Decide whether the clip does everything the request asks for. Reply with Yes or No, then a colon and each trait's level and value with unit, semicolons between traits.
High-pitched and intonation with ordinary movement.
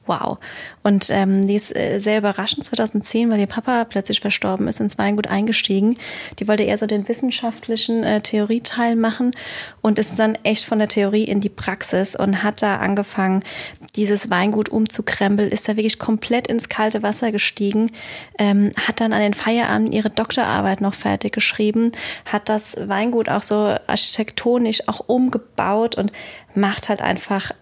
No: high, 215 Hz; narrow, 1.8 semitones